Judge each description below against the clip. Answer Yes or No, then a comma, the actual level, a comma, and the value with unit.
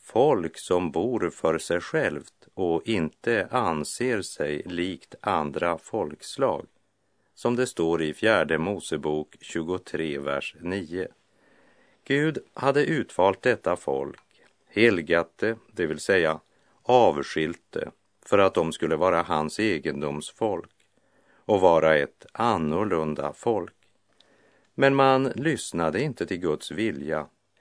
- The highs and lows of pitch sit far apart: Yes, wide, 7.7 semitones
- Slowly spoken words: Yes, slow, 110 wpm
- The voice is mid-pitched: No, very low, 85 Hz